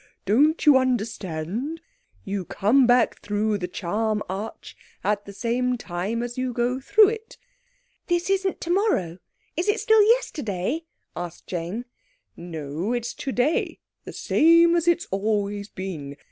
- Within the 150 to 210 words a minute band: No, slow, 135 wpm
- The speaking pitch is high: Yes, high, 230 Hz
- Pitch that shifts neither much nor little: No, wide, 7.8 semitones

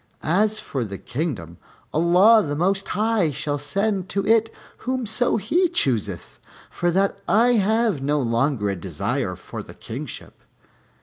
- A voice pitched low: No, medium, 185 Hz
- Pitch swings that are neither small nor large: No, wide, 7.4 semitones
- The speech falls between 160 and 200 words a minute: No, average, 140 wpm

